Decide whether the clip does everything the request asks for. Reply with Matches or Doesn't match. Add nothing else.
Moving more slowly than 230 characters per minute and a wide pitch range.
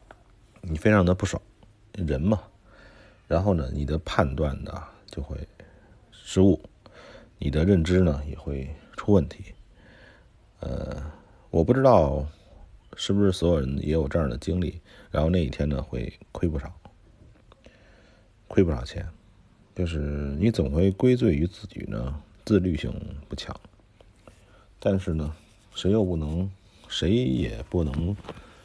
Doesn't match